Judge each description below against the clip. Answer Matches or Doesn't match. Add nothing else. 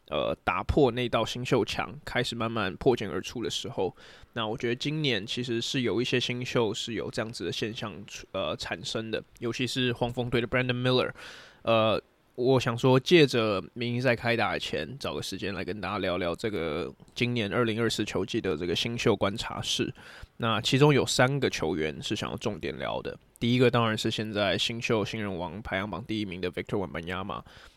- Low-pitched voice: Matches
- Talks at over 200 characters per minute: Matches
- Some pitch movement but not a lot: Matches